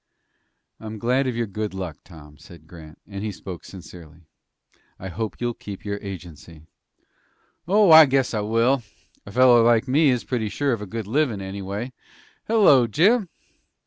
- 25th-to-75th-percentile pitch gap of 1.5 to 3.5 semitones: No, average, 5.1 semitones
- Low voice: Yes, low, 110 Hz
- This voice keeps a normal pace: Yes, average, 165 wpm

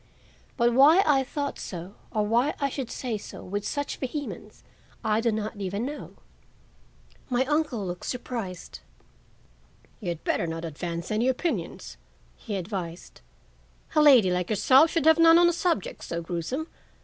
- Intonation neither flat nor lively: No, wide, 7.5 semitones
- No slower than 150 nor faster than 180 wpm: Yes, average, 160 wpm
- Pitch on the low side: No, high, 235 Hz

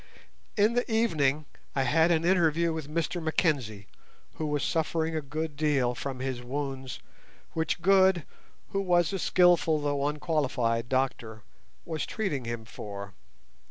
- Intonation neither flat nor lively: Yes, average, 4.3 semitones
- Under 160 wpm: Yes, average, 140 wpm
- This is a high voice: No, medium, 150 Hz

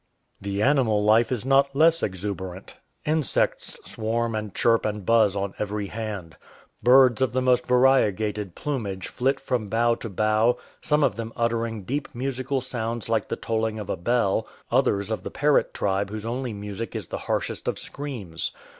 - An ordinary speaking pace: Yes, average, 170 wpm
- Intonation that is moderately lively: Yes, average, 3.7 semitones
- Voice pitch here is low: Yes, low, 115 Hz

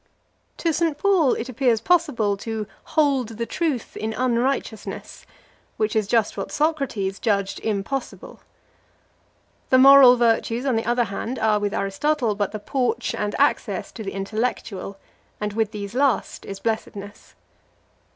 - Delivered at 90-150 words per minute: Yes, average, 140 wpm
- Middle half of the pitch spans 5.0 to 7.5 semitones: No, average, 4.4 semitones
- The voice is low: No, high, 230 Hz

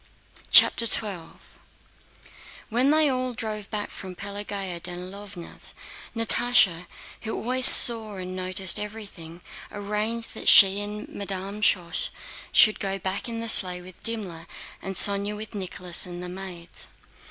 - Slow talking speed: Yes, slow, 130 wpm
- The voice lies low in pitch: No, high, 200 Hz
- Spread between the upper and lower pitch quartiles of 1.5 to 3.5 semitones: Yes, average, 3.0 semitones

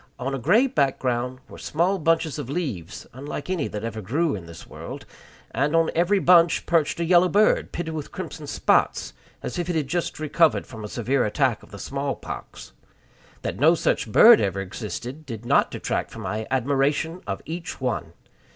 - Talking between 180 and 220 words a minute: Yes, average, 190 wpm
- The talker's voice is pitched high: No, medium, 140 Hz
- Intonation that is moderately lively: No, wide, 6.0 semitones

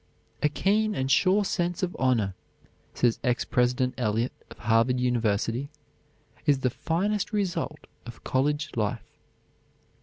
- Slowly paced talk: Yes, slow, 125 wpm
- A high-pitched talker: No, low, 130 Hz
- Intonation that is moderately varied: No, wide, 6.6 semitones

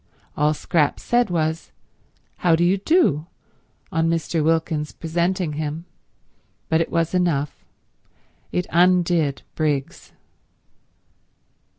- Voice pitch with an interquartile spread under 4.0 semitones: Yes, narrow, 2.4 semitones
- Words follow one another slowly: Yes, slow, 100 wpm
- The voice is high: No, medium, 165 Hz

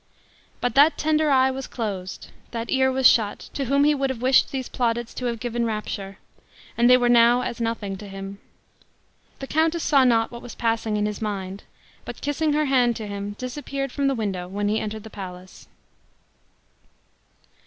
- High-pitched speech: Yes, high, 235 Hz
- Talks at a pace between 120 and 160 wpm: No, average, 185 wpm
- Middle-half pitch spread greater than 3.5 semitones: Yes, average, 4.2 semitones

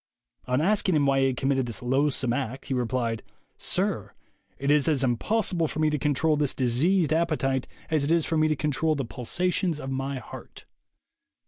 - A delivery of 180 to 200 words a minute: Yes, average, 190 wpm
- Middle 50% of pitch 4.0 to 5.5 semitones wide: No, average, 3.2 semitones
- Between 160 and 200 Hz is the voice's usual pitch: No, medium, 140 Hz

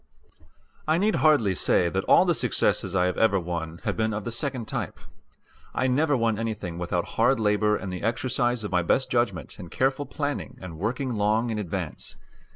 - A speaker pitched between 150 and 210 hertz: No, low, 110 Hz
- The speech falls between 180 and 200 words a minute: Yes, average, 190 wpm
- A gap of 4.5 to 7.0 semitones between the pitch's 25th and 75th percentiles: Yes, wide, 5.5 semitones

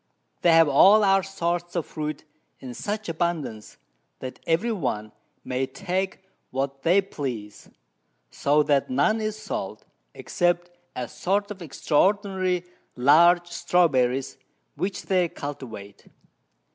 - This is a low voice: No, medium, 170 Hz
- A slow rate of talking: Yes, slow, 120 wpm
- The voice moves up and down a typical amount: No, wide, 5.7 semitones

